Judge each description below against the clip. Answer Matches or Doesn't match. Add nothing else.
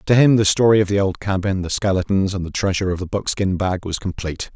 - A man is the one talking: Matches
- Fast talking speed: Matches